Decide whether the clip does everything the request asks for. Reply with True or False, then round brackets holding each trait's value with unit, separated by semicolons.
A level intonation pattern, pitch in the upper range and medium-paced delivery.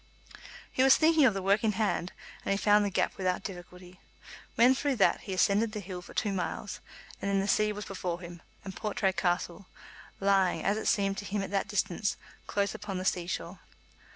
False (2.2 semitones; 195 Hz; 210 wpm)